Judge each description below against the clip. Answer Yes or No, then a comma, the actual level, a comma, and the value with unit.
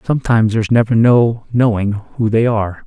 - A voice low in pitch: Yes, low, 115 Hz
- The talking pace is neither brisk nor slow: Yes, average, 165 wpm